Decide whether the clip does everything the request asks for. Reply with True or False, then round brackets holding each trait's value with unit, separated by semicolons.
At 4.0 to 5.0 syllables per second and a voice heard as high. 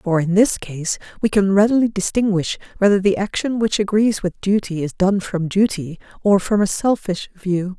True (4.8 syllables/s; 195 Hz)